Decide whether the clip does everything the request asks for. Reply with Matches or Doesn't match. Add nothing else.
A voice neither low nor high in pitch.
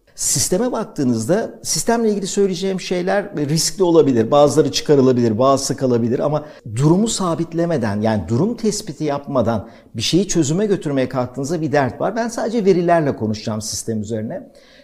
Matches